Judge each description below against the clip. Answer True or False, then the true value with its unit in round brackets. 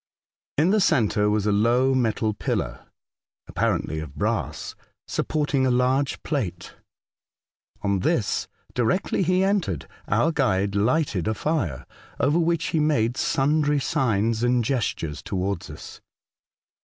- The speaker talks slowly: True (125 wpm)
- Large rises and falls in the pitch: True (6.3 semitones)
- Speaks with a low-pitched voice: True (125 Hz)